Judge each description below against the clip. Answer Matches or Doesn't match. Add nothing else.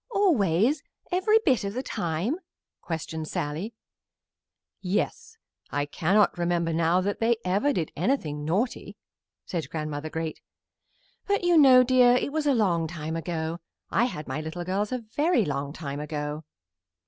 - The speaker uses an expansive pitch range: Matches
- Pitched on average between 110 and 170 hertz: Doesn't match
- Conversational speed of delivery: Matches